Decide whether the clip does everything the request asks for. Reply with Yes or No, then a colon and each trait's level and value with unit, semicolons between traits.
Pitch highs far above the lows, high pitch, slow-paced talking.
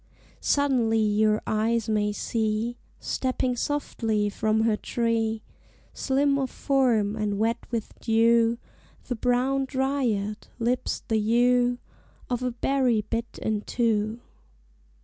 No: narrow, 2.5 semitones; high, 230 Hz; slow, 110 wpm